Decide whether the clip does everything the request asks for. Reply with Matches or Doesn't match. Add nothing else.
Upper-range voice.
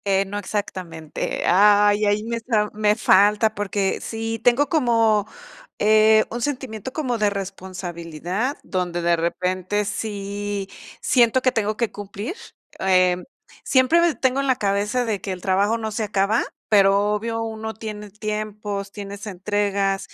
Matches